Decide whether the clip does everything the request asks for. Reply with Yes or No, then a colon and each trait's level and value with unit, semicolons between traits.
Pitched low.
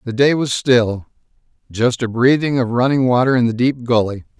Yes: low, 125 Hz